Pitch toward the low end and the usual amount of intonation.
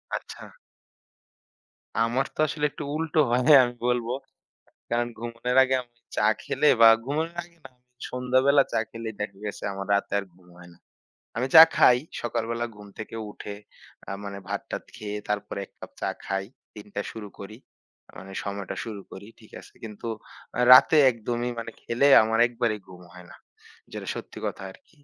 Yes: low, 115 Hz; average, 3.5 semitones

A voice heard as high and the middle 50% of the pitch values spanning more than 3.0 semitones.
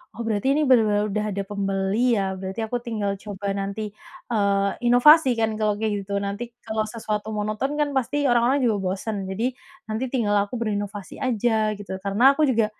No: high, 215 Hz; average, 2.7 semitones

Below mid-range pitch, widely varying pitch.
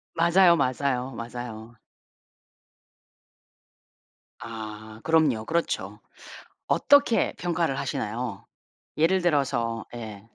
Yes: low, 125 Hz; wide, 6.5 semitones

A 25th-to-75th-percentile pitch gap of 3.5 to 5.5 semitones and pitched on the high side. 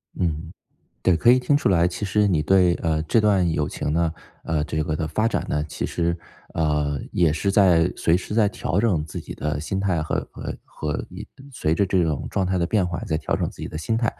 No: average, 4.0 semitones; very low, 85 Hz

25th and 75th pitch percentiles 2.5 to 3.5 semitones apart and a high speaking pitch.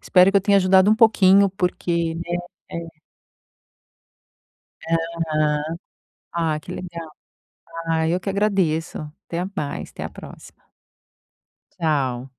No: average, 2.8 semitones; medium, 170 Hz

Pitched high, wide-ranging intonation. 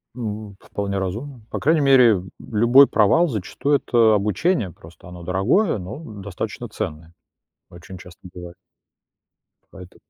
No: low, 105 Hz; wide, 5.8 semitones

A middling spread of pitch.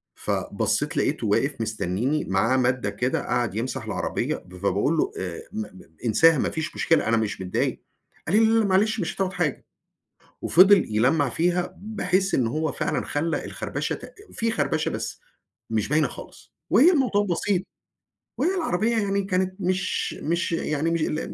No: wide, 8.0 semitones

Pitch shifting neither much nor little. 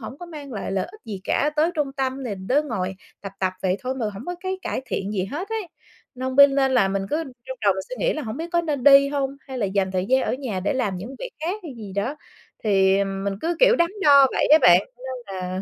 No: wide, 6.9 semitones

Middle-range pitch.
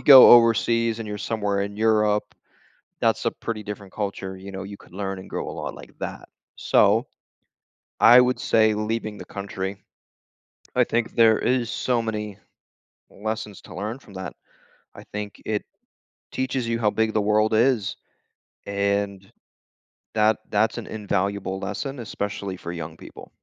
No: low, 105 Hz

